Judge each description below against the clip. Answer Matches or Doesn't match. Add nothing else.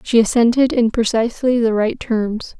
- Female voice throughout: Matches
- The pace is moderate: Matches